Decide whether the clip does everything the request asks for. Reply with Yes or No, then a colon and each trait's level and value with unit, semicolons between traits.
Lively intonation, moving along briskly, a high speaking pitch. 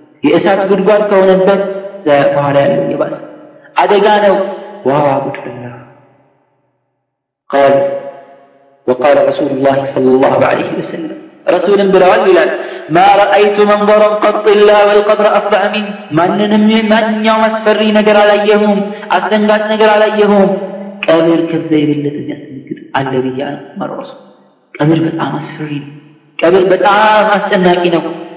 Yes: wide, 6.3 semitones; fast, 115 wpm; high, 195 Hz